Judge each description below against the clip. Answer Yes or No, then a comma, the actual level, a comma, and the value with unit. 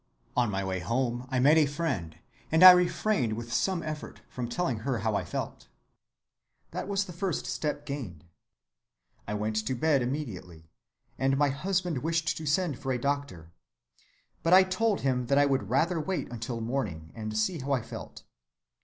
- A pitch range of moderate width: No, wide, 6.2 semitones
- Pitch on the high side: No, low, 135 Hz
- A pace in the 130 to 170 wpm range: No, average, 180 wpm